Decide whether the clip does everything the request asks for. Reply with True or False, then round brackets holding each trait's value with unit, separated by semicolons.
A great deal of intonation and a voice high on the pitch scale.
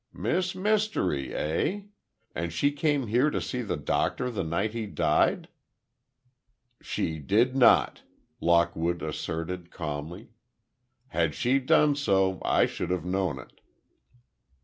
False (7.9 semitones; 95 Hz)